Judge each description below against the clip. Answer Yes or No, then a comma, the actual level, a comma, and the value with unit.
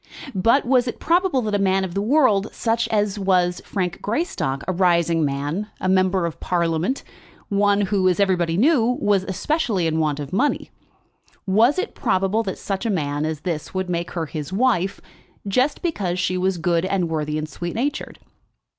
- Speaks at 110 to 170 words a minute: No, average, 180 wpm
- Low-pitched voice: No, high, 190 Hz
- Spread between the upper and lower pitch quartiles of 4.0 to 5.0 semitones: Yes, average, 4.3 semitones